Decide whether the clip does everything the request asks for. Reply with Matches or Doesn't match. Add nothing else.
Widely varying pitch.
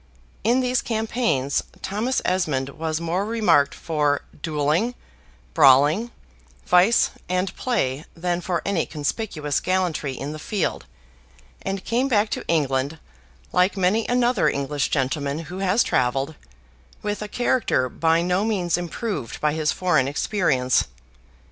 Matches